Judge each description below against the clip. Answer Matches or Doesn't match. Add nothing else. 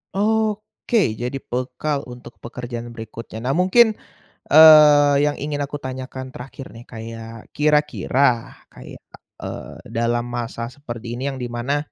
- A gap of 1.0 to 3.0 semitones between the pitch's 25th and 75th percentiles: Doesn't match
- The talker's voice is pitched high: Doesn't match